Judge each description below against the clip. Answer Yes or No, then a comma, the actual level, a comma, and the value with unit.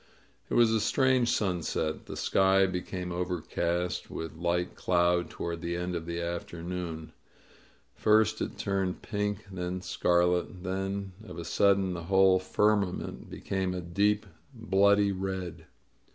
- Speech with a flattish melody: Yes, narrow, 2.3 semitones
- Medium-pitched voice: No, very low, 90 Hz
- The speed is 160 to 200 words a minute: No, slow, 135 wpm